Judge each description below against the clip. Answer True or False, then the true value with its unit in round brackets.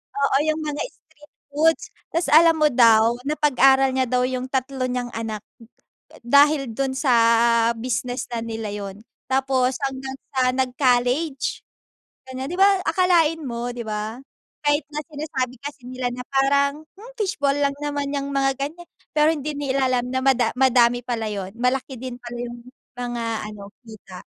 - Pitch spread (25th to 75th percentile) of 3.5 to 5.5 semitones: False (2.9 semitones)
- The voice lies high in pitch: True (260 Hz)